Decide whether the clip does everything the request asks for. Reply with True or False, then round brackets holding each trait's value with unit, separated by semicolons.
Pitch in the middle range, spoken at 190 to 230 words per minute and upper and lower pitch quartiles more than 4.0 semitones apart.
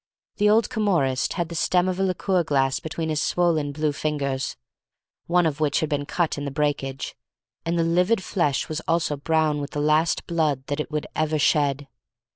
False (155 Hz; 195 wpm; 2.9 semitones)